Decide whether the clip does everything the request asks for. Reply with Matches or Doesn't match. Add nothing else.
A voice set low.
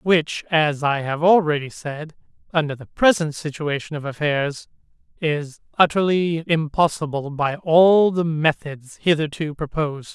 Doesn't match